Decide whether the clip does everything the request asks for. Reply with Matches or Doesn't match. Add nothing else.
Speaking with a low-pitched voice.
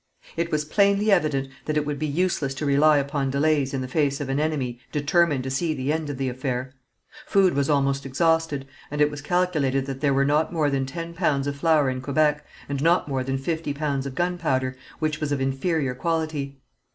Doesn't match